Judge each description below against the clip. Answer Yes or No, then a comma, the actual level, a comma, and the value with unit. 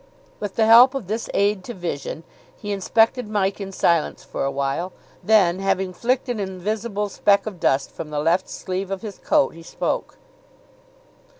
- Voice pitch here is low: No, high, 195 Hz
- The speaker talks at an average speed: Yes, average, 175 wpm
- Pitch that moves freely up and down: No, average, 3.5 semitones